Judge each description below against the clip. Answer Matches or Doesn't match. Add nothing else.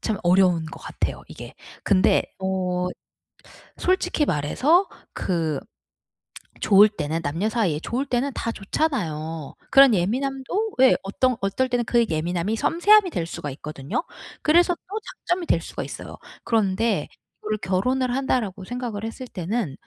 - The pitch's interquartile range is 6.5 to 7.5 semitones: Matches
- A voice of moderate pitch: Doesn't match